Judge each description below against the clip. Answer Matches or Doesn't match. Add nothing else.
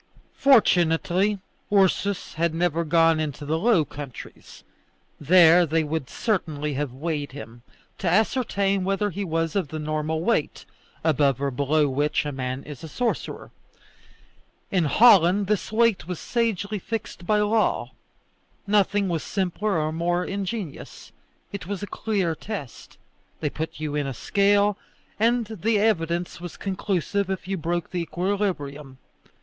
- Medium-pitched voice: Matches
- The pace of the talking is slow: Doesn't match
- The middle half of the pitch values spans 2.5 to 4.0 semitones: Doesn't match